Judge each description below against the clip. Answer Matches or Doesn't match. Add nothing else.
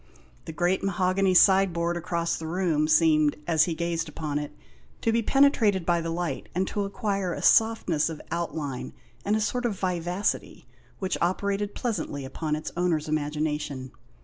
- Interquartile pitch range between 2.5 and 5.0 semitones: Matches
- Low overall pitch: Doesn't match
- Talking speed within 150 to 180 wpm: Matches